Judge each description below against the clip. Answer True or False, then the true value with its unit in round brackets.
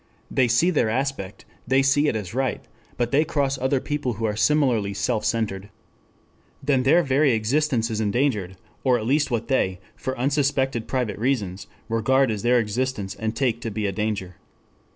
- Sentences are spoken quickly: False (175 wpm)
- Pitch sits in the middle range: False (120 Hz)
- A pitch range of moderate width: True (4.0 semitones)